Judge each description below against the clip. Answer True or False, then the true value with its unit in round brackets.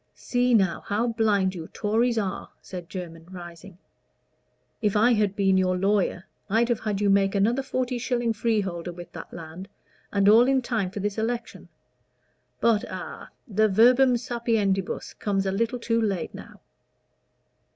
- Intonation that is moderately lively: True (3.4 semitones)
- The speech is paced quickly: False (155 wpm)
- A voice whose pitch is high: True (210 Hz)